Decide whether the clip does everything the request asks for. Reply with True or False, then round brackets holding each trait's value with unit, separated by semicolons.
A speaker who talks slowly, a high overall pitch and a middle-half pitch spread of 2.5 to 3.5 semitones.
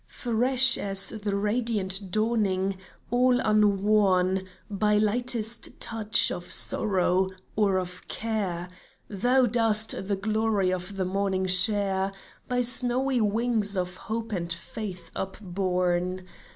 True (115 wpm; 205 Hz; 3.1 semitones)